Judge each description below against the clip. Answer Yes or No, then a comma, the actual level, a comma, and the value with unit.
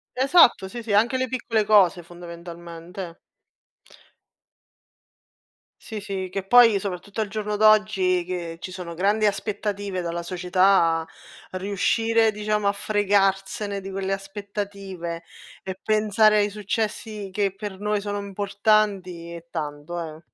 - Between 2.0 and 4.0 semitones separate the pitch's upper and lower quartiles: Yes, average, 2.7 semitones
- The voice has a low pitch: No, high, 200 Hz